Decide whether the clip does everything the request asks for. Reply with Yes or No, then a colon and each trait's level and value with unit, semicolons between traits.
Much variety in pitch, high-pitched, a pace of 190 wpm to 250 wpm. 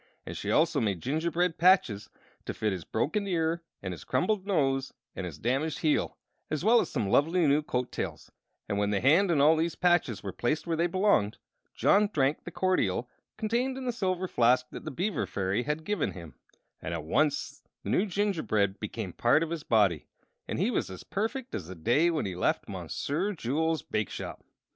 No: wide, 8.9 semitones; medium, 150 Hz; average, 195 wpm